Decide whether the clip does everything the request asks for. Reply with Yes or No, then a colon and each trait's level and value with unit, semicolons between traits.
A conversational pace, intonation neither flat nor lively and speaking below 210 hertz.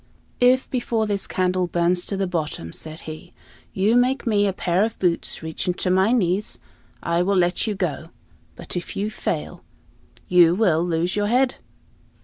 Yes: average, 170 wpm; average, 3.6 semitones; medium, 185 Hz